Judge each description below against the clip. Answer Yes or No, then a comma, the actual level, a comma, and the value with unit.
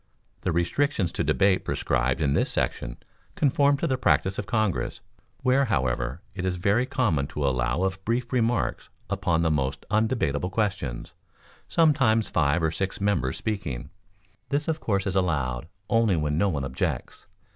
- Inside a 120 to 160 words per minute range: Yes, average, 155 wpm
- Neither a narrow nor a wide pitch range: No, wide, 7.7 semitones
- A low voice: Yes, very low, 95 Hz